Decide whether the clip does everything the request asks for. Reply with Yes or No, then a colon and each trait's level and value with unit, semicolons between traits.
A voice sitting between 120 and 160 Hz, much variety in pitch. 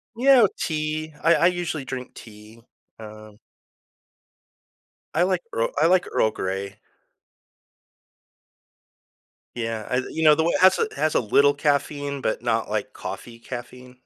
Yes: medium, 140 Hz; wide, 6.0 semitones